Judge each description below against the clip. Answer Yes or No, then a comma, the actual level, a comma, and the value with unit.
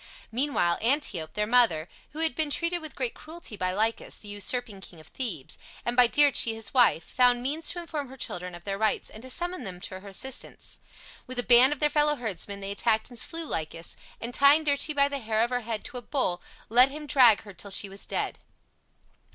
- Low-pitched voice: No, high, 245 Hz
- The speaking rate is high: Yes, fast, 220 wpm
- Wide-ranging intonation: Yes, wide, 5.9 semitones